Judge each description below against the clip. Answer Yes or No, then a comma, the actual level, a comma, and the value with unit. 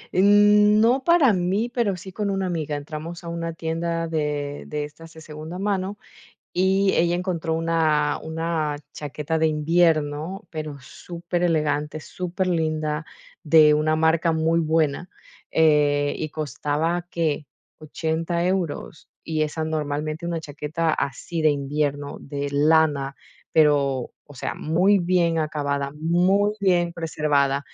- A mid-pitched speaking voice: Yes, medium, 160 Hz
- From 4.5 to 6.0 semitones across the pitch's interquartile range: No, average, 2.7 semitones